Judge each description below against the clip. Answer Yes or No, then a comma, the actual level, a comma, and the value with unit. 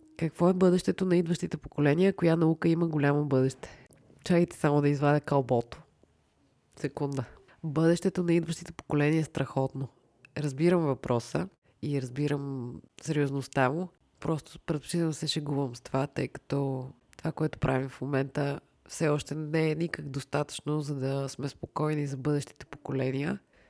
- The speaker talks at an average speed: Yes, average, 140 wpm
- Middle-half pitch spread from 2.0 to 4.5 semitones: Yes, average, 3.0 semitones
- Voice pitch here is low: No, medium, 145 Hz